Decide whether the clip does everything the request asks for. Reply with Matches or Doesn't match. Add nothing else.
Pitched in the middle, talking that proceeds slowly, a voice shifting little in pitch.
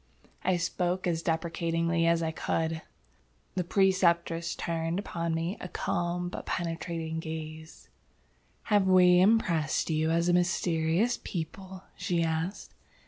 Matches